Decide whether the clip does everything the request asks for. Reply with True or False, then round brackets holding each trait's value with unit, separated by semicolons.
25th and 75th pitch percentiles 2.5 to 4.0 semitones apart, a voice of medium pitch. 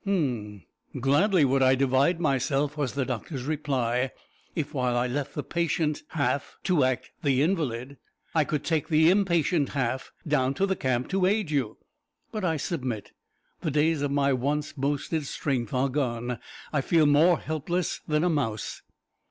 True (3.5 semitones; 145 Hz)